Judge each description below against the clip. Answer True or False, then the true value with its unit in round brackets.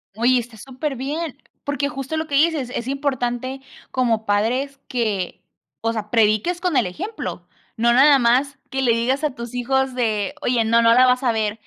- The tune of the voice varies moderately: True (3.2 semitones)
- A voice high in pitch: True (250 Hz)